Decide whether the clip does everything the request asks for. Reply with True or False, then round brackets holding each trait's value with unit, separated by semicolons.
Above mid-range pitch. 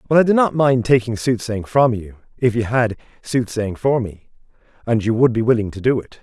False (120 Hz)